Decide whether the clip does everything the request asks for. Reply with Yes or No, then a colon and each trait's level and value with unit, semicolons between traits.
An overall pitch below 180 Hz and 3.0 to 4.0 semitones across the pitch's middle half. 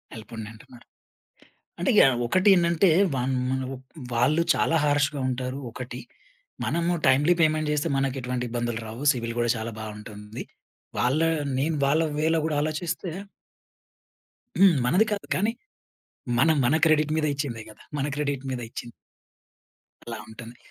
No: low, 135 Hz; average, 4.6 semitones